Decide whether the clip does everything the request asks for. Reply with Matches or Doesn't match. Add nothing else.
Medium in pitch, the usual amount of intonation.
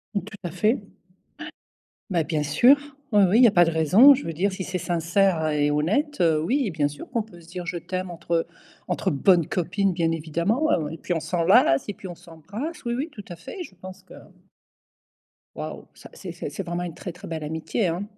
Matches